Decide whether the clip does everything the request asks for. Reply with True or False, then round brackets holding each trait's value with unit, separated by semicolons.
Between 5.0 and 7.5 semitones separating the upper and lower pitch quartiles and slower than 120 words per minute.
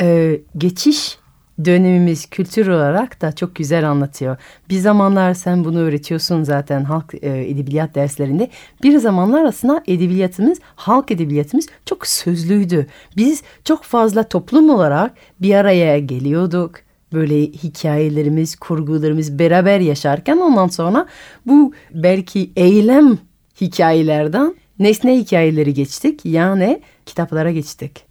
True (5.5 semitones; 110 wpm)